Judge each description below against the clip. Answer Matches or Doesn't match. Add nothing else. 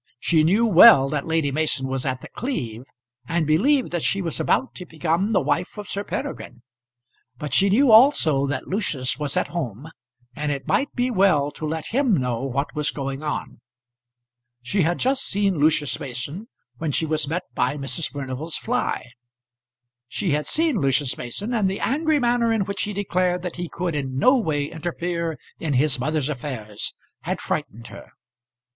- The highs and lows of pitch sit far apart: Matches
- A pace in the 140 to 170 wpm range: Doesn't match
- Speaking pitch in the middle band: Matches